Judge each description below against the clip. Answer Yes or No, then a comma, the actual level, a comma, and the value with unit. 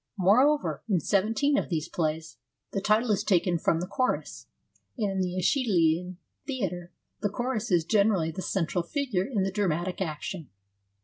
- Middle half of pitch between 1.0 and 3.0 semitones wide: No, average, 3.9 semitones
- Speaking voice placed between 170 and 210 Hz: Yes, high, 190 Hz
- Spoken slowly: No, average, 165 wpm